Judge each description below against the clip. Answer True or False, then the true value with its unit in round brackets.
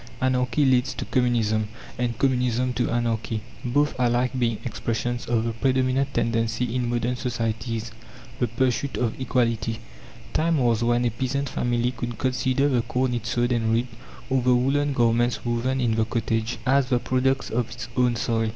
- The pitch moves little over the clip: True (1.8 semitones)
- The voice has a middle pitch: False (120 Hz)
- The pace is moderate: True (170 wpm)